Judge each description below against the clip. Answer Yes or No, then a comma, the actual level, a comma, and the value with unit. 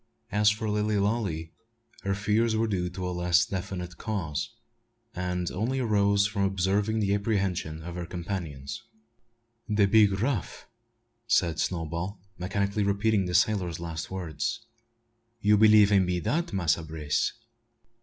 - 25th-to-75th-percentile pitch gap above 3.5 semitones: No, average, 3.2 semitones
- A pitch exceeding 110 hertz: No, low, 100 Hz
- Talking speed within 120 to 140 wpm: Yes, slow, 135 wpm